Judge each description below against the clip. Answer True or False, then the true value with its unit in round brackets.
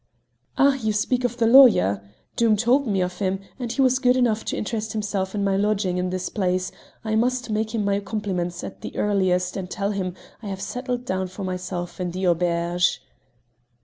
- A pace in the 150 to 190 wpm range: False (205 wpm)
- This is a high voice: True (200 Hz)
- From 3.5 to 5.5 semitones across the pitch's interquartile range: True (3.8 semitones)